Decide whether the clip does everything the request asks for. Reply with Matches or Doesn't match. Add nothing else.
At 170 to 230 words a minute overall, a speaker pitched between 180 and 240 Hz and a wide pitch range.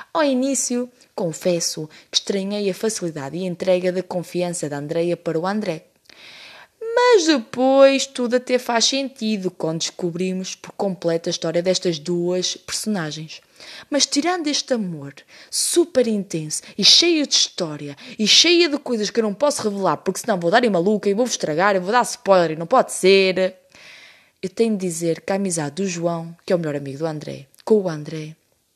Matches